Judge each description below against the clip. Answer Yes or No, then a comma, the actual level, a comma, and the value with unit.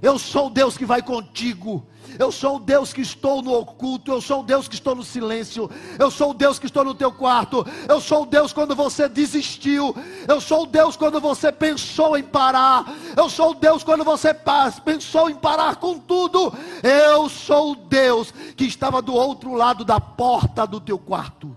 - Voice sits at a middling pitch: No, very high, 275 Hz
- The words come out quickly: Yes, fast, 205 wpm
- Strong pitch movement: No, average, 3.2 semitones